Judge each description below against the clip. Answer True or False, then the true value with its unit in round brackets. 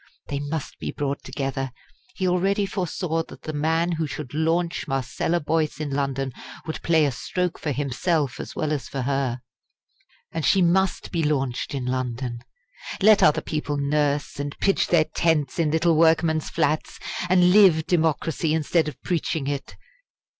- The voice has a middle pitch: True (155 Hz)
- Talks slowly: False (160 wpm)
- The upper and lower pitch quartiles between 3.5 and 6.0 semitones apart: False (3.1 semitones)